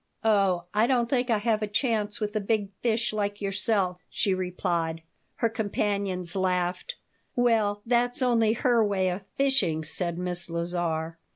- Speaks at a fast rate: No, average, 155 wpm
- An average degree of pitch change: Yes, average, 4.0 semitones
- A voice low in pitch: No, high, 205 Hz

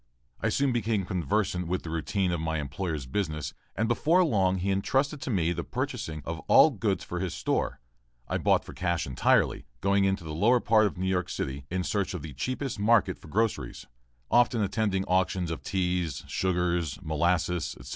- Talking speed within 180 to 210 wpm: Yes, average, 185 wpm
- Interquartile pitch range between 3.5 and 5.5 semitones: Yes, average, 4.1 semitones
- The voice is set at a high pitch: No, very low, 90 Hz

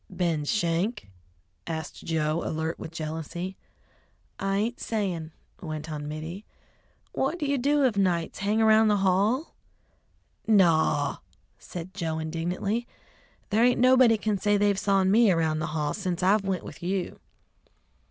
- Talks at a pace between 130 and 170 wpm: Yes, average, 145 wpm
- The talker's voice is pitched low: No, medium, 185 Hz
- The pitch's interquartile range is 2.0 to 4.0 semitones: No, average, 4.9 semitones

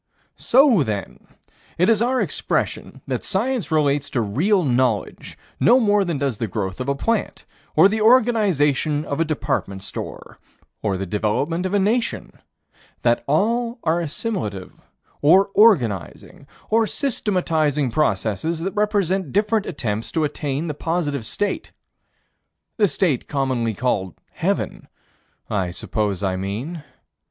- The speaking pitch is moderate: Yes, medium, 155 Hz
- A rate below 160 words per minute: Yes, slow, 135 wpm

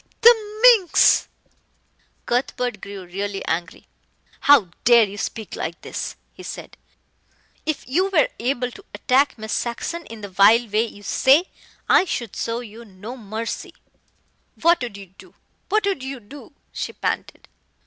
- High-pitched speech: Yes, high, 235 Hz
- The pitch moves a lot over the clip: Yes, wide, 6.1 semitones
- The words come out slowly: No, average, 150 wpm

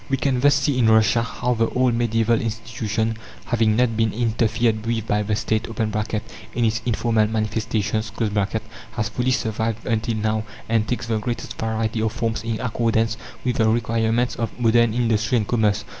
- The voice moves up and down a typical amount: No, narrow, 1.3 semitones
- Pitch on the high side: No, low, 115 Hz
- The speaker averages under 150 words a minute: No, average, 170 wpm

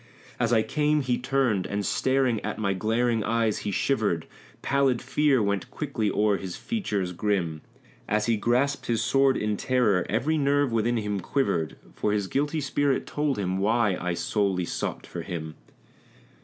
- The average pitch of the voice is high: No, low, 110 Hz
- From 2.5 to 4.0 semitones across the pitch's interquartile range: No, average, 5.2 semitones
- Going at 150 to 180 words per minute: Yes, average, 165 wpm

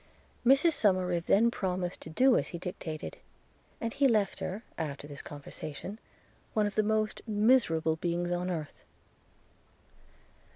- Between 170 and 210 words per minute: No, slow, 135 wpm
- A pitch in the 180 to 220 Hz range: Yes, medium, 185 Hz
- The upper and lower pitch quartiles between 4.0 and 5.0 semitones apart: Yes, average, 4.5 semitones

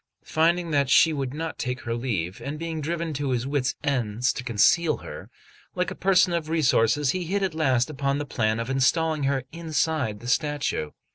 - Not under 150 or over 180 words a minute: No, average, 195 wpm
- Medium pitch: Yes, medium, 145 Hz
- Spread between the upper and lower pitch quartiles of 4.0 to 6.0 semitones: Yes, average, 4.3 semitones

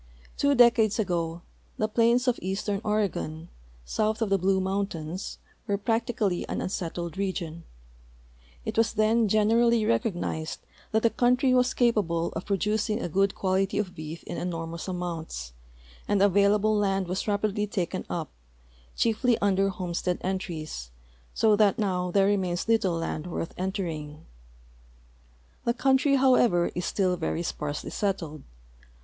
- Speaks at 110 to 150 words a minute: Yes, average, 140 wpm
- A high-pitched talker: Yes, high, 195 Hz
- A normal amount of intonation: Yes, average, 3.8 semitones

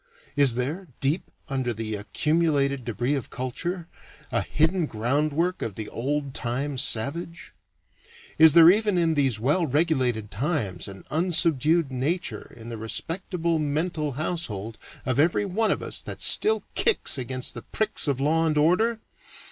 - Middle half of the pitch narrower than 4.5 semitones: No, average, 5.2 semitones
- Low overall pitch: No, medium, 145 Hz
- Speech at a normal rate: Yes, average, 150 wpm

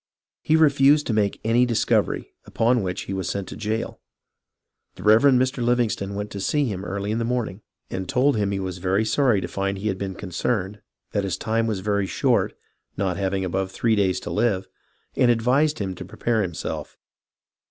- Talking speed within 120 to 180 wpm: No, average, 195 wpm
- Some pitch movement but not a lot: Yes, average, 3.7 semitones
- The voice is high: No, low, 105 Hz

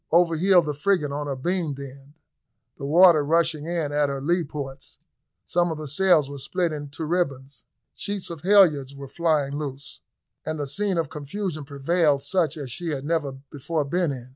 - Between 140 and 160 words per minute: No, average, 185 wpm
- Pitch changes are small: No, average, 3.5 semitones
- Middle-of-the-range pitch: Yes, medium, 150 Hz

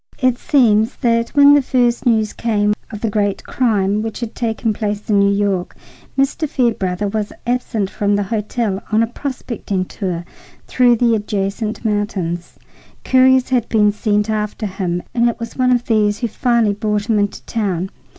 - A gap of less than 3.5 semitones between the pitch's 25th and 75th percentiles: Yes, average, 2.7 semitones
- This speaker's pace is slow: No, average, 170 wpm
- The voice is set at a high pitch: Yes, high, 215 Hz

